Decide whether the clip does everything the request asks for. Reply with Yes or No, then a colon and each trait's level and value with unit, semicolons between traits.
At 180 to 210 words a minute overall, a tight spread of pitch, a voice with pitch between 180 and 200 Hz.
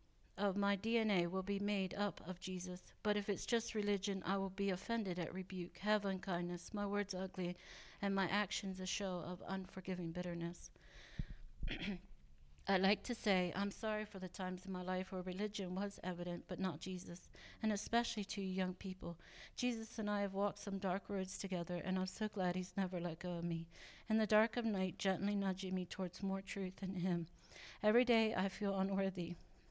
Yes: average, 190 wpm; narrow, 2.0 semitones; high, 190 Hz